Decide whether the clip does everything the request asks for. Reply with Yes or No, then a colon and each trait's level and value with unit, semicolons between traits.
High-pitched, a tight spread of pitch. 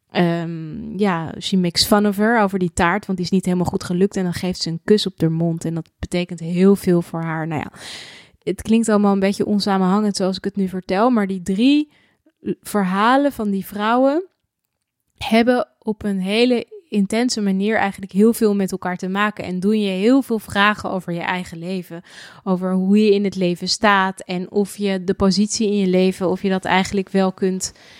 Yes: high, 195 Hz; narrow, 2.3 semitones